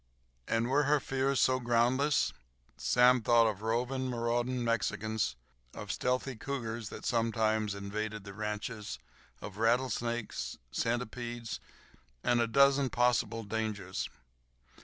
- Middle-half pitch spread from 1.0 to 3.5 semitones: Yes, narrow, 2.4 semitones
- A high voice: No, low, 115 Hz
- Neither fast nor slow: No, slow, 115 wpm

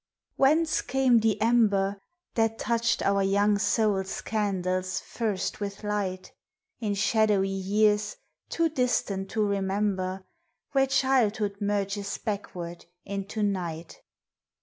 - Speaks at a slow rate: Yes, slow, 105 wpm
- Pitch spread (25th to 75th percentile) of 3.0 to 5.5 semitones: No, narrow, 2.5 semitones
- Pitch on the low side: No, high, 205 Hz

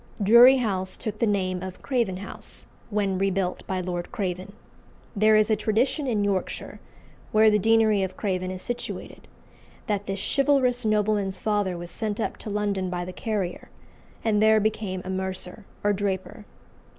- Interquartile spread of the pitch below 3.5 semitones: Yes, narrow, 2.6 semitones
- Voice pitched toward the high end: Yes, high, 205 Hz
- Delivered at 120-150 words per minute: No, average, 165 wpm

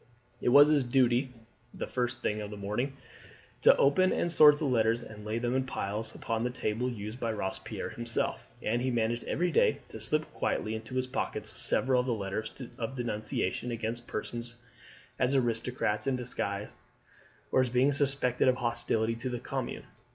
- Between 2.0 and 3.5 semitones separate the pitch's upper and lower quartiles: Yes, narrow, 2.6 semitones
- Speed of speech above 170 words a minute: Yes, average, 180 wpm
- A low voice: Yes, low, 120 Hz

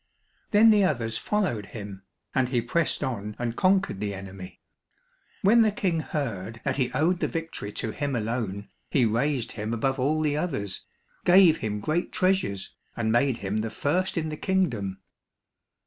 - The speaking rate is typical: Yes, average, 165 wpm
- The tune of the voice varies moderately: No, wide, 7.6 semitones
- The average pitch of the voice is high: No, low, 125 Hz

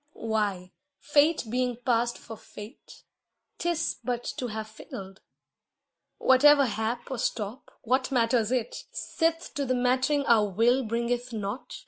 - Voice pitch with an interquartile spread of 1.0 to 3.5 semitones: Yes, average, 3.1 semitones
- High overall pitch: Yes, high, 240 Hz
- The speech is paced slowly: Yes, slow, 130 wpm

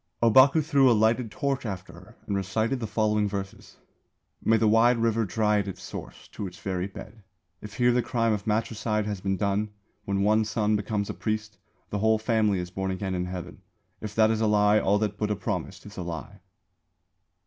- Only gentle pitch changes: Yes, narrow, 2.3 semitones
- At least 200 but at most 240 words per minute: Yes, fast, 205 wpm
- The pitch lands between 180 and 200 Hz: No, low, 105 Hz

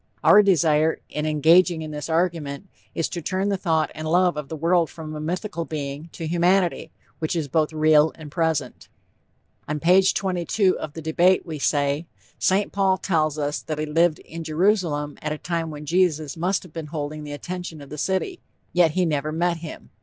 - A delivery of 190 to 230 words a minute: Yes, average, 195 wpm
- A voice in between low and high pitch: Yes, medium, 160 Hz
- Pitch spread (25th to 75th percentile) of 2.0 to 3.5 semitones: Yes, average, 2.7 semitones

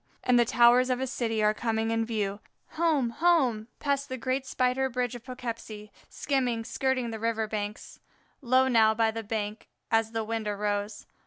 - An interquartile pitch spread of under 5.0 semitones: Yes, average, 2.7 semitones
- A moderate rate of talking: Yes, average, 175 wpm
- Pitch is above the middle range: Yes, high, 230 Hz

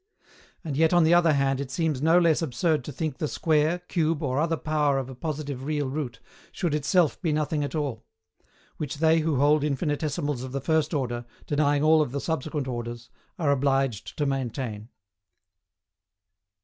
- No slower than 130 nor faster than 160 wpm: No, average, 175 wpm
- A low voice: No, medium, 145 Hz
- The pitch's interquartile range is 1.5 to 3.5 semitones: Yes, average, 2.8 semitones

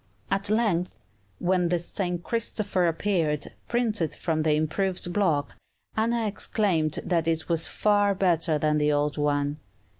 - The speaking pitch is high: No, medium, 175 Hz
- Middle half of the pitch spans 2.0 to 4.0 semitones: No, average, 4.6 semitones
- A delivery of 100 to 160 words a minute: Yes, average, 140 wpm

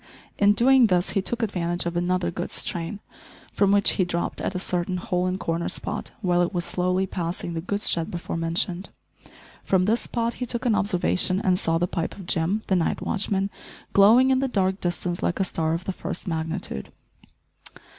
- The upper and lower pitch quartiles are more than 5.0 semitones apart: No, average, 2.7 semitones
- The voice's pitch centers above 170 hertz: Yes, medium, 185 Hz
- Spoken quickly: No, average, 195 wpm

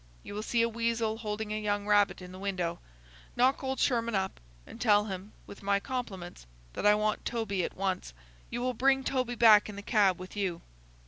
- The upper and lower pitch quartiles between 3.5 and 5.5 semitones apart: No, average, 3.0 semitones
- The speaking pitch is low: No, high, 210 Hz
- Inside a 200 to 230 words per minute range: Yes, fast, 205 wpm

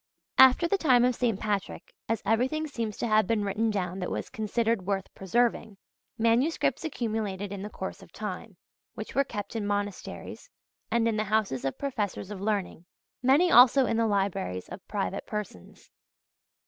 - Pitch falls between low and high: No, high, 215 Hz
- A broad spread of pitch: No, average, 3.2 semitones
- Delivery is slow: No, average, 170 wpm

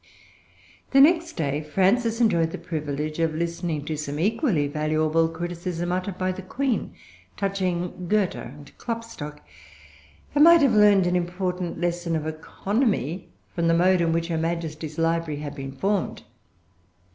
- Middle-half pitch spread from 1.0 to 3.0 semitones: No, average, 3.7 semitones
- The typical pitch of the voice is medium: Yes, medium, 170 Hz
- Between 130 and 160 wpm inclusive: Yes, average, 145 wpm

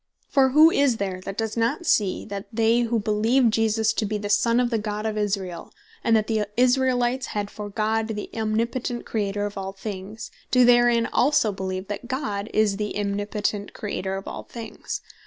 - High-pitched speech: Yes, high, 215 Hz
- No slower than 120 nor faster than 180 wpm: No, average, 190 wpm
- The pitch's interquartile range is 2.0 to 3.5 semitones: Yes, narrow, 2.6 semitones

